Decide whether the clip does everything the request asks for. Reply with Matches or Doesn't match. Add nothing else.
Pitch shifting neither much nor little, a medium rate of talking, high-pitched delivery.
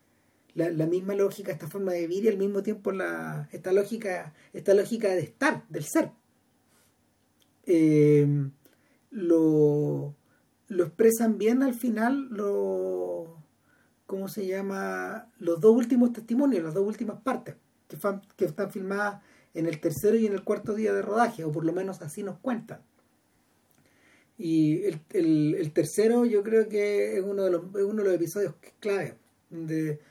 Matches